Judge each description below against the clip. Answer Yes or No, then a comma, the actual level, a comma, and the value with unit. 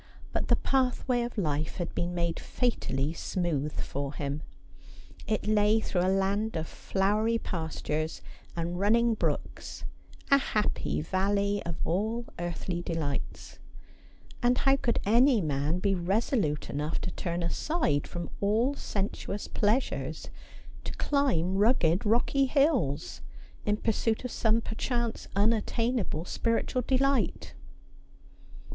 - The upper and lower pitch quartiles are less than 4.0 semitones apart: No, wide, 5.6 semitones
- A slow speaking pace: Yes, slow, 120 wpm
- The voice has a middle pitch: No, high, 205 Hz